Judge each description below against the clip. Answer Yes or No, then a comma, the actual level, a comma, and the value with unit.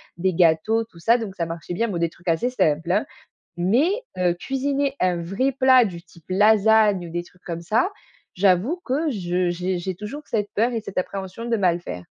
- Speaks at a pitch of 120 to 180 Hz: No, high, 190 Hz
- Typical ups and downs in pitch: Yes, average, 4.9 semitones